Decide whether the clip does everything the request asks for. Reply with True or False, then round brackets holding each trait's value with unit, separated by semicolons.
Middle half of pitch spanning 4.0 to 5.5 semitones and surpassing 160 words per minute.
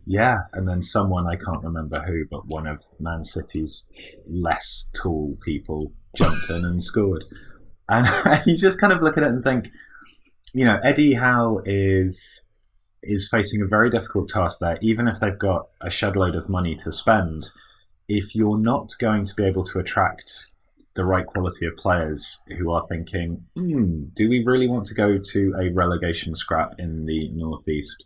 True (4.5 semitones; 180 wpm)